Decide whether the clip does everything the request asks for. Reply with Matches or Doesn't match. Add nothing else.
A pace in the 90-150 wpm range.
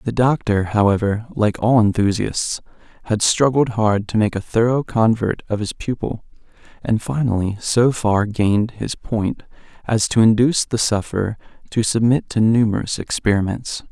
Matches